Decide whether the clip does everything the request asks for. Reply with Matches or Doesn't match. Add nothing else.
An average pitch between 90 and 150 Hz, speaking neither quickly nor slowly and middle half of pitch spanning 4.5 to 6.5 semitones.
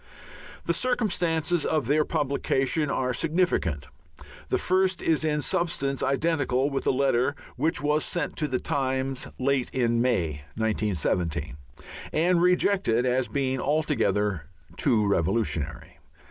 Doesn't match